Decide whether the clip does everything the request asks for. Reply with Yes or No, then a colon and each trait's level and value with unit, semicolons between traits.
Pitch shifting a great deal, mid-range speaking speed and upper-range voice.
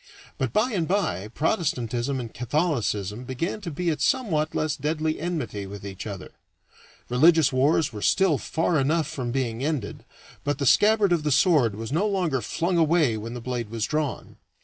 No: wide, 5.9 semitones; average, 175 wpm; medium, 145 Hz